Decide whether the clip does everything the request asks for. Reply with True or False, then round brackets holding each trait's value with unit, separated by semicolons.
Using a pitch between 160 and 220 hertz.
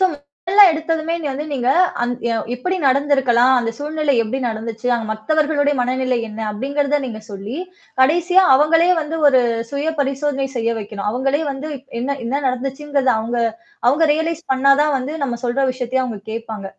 False (270 Hz)